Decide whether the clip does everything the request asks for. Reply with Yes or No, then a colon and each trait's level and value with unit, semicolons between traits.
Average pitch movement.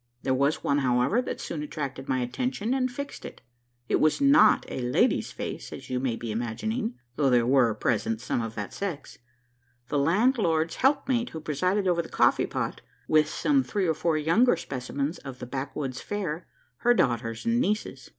No: wide, 8.7 semitones